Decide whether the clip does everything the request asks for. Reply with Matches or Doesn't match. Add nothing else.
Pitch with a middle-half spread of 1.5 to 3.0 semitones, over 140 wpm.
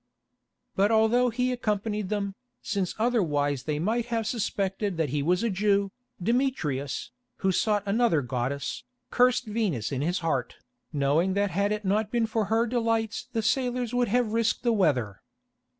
Doesn't match